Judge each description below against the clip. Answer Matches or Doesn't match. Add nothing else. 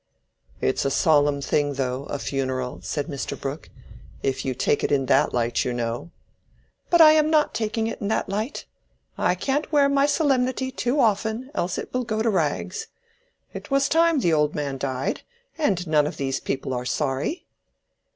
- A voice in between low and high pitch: Matches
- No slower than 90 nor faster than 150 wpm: Doesn't match